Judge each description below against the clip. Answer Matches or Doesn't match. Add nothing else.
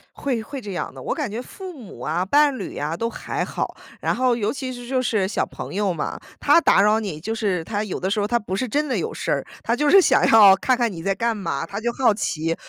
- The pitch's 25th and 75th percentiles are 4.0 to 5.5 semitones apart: Matches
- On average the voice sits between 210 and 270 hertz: Matches